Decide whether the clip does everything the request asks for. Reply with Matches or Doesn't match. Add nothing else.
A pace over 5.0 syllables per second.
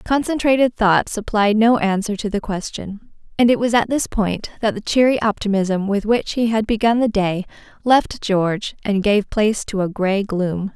Doesn't match